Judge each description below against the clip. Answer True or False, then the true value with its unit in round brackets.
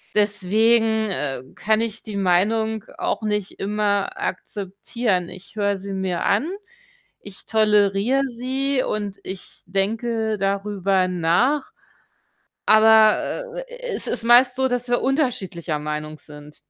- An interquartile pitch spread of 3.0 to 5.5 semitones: True (3.4 semitones)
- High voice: True (210 Hz)